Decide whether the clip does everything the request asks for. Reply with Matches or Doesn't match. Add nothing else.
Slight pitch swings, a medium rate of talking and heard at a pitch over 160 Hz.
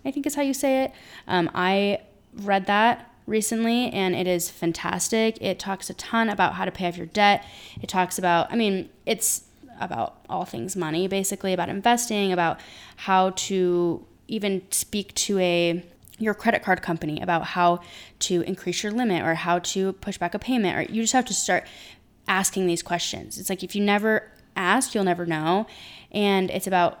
Doesn't match